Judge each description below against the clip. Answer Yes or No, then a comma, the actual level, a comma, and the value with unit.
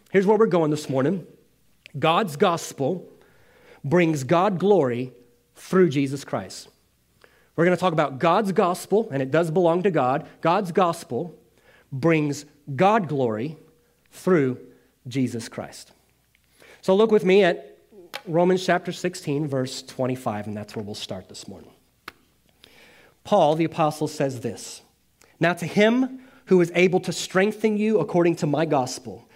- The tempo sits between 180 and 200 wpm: No, average, 145 wpm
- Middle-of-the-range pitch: Yes, medium, 165 Hz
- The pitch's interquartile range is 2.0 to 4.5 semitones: No, average, 5.2 semitones